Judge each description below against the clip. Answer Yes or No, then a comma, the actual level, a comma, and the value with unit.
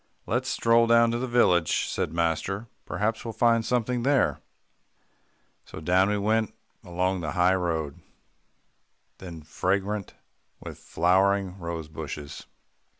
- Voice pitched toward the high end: No, very low, 95 Hz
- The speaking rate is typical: No, slow, 120 wpm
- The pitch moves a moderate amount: Yes, average, 5.0 semitones